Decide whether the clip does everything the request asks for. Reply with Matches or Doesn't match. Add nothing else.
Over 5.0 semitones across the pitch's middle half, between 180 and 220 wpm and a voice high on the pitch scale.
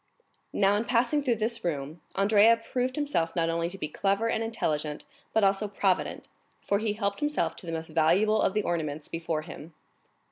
Matches